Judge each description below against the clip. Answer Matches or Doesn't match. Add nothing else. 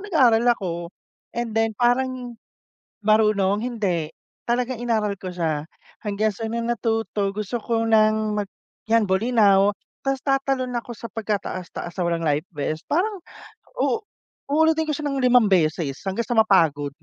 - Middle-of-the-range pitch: Doesn't match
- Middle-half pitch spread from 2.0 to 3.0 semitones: Doesn't match